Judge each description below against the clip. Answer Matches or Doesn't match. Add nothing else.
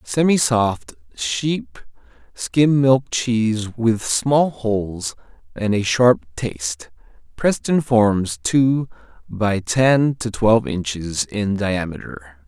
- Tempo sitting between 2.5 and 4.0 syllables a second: Matches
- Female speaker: Doesn't match